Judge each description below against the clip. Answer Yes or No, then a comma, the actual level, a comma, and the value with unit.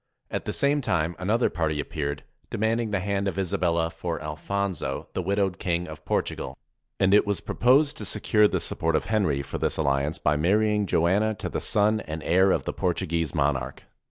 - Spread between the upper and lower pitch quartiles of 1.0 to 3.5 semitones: No, average, 4.7 semitones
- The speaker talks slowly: No, average, 185 wpm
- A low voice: Yes, very low, 90 Hz